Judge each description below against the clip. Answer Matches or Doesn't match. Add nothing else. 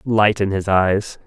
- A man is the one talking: Matches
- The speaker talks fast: Doesn't match